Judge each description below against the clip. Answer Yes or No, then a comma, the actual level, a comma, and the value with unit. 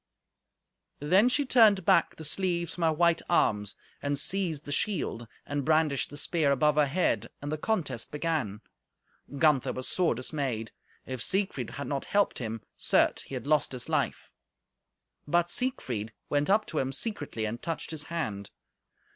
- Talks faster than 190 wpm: No, average, 165 wpm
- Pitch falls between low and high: Yes, medium, 150 Hz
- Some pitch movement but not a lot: Yes, average, 5.0 semitones